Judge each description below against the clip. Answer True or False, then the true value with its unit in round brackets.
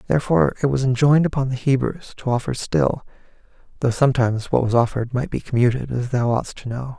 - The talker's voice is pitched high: False (130 Hz)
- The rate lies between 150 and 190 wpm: False (200 wpm)